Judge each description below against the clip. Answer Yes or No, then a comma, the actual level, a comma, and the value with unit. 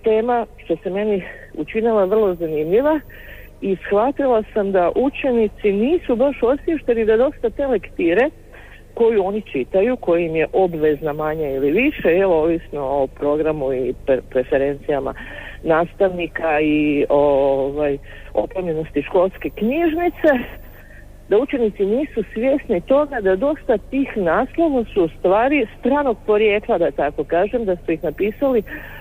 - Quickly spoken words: No, average, 130 wpm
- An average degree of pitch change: No, wide, 8.0 semitones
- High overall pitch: Yes, high, 200 Hz